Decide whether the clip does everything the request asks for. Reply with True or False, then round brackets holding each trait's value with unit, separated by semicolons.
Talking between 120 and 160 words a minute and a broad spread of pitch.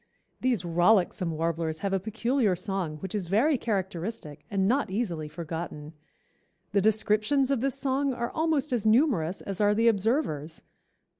True (150 wpm; 5.8 semitones)